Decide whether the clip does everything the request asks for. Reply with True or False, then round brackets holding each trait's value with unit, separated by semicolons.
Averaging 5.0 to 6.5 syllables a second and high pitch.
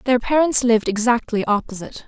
True (5.9 syllables/s; 235 Hz)